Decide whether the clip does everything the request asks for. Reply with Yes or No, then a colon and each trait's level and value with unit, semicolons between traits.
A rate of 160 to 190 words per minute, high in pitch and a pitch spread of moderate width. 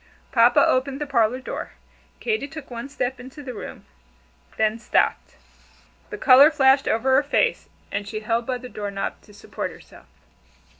Yes: average, 165 wpm; very high, 255 Hz; average, 3.4 semitones